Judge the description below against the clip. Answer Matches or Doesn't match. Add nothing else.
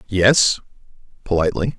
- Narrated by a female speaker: Doesn't match